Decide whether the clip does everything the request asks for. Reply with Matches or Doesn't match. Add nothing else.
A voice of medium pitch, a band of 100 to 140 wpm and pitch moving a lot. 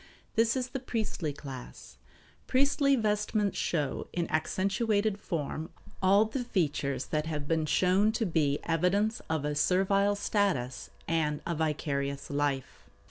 Matches